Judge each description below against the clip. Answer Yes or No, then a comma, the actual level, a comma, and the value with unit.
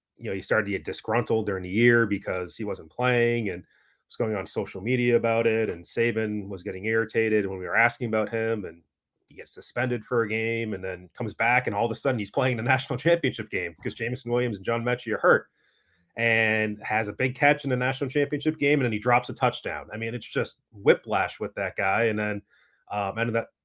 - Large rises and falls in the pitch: No, narrow, 2.5 semitones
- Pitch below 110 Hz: No, low, 115 Hz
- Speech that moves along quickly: Yes, fast, 235 wpm